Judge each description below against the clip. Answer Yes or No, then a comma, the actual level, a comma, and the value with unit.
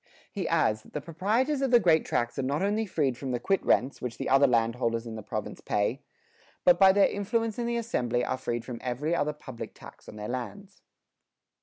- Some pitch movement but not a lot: No, wide, 8.5 semitones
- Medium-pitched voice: Yes, medium, 145 Hz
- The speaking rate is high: Yes, fast, 215 wpm